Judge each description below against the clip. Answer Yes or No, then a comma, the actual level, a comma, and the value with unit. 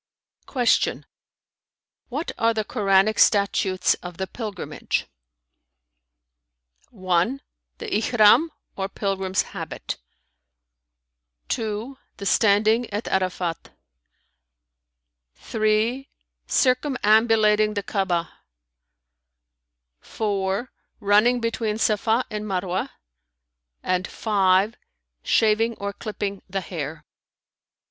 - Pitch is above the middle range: Yes, high, 210 Hz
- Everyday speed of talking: No, slow, 80 wpm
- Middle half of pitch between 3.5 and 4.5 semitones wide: No, average, 2.9 semitones